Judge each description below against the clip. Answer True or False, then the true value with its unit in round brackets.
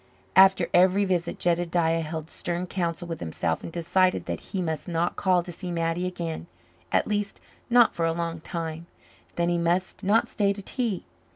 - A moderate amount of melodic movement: False (2.1 semitones)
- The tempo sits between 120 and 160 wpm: False (180 wpm)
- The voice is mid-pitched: True (175 Hz)